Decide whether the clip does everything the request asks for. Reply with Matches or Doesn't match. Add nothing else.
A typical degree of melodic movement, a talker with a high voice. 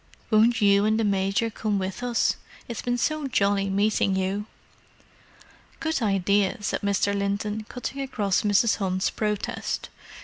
Doesn't match